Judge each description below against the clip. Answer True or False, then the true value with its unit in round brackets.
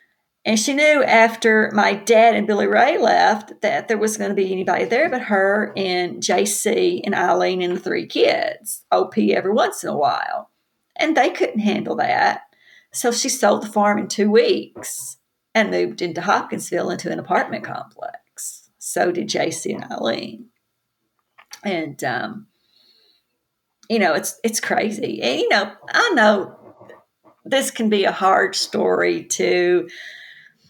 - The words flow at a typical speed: True (155 wpm)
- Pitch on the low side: False (210 Hz)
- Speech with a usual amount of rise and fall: True (4.2 semitones)